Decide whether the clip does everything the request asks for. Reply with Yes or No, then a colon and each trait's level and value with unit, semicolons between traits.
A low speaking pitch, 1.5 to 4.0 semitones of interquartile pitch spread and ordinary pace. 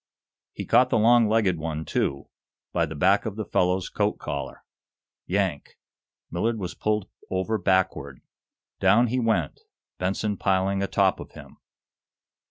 Yes: very low, 95 Hz; average, 3.6 semitones; average, 145 wpm